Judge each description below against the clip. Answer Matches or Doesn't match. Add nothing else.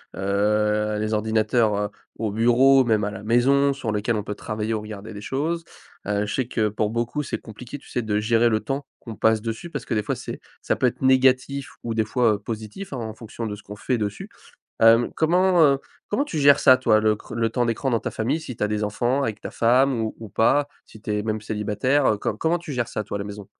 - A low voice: Matches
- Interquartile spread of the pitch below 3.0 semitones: Doesn't match